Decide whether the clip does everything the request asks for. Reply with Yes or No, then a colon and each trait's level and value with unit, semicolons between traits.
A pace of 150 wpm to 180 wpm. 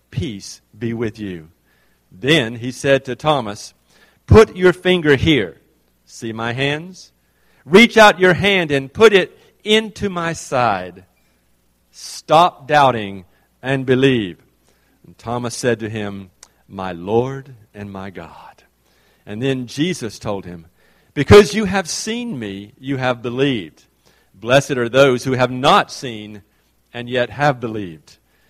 No: slow, 135 wpm